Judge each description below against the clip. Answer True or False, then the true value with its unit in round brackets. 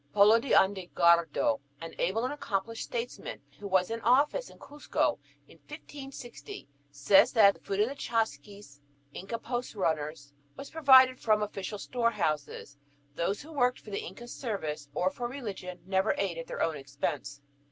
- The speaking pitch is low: False (205 Hz)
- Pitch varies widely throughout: True (6.1 semitones)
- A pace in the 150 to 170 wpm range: True (160 wpm)